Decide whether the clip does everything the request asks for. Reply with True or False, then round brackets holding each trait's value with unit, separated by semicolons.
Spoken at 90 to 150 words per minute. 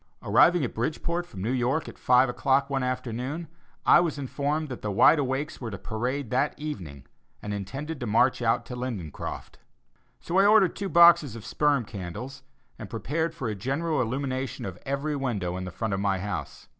False (190 wpm)